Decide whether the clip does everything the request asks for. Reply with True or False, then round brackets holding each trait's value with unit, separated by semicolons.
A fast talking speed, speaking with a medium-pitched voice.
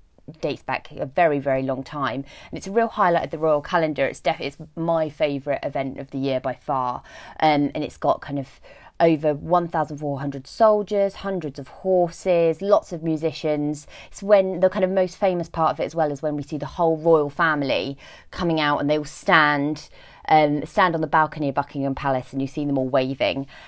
True (215 wpm; 150 Hz)